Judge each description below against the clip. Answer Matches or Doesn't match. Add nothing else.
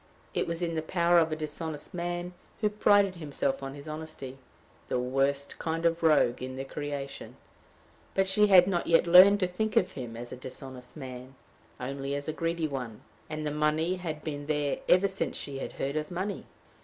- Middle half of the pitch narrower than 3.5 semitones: Doesn't match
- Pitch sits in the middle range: Matches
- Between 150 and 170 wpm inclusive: Doesn't match